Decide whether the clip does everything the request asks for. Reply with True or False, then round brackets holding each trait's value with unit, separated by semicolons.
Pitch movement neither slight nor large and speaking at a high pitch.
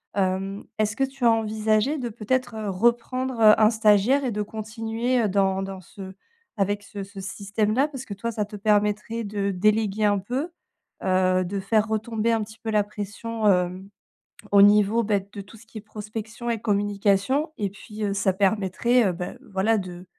False (2.2 semitones; 210 Hz)